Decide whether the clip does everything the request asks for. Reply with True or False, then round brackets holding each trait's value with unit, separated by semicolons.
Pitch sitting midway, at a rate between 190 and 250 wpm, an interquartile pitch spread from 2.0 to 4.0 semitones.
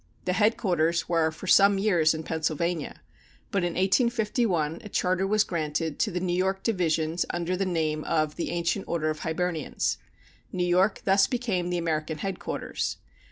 False (175 Hz; 160 wpm; 3.2 semitones)